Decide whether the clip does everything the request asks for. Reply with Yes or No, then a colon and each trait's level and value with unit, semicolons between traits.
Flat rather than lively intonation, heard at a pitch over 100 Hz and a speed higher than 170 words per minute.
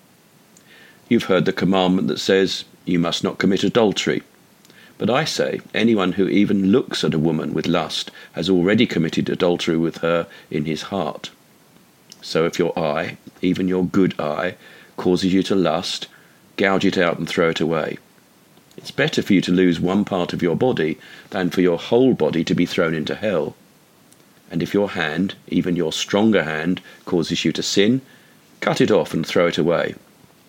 No: narrow, 1.7 semitones; very low, 90 Hz; average, 180 wpm